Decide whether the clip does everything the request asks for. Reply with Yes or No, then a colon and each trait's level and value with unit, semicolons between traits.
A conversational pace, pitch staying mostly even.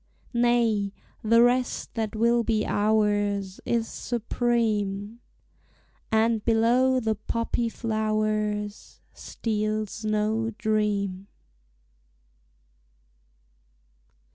No: slow, 70 wpm; narrow, 1.8 semitones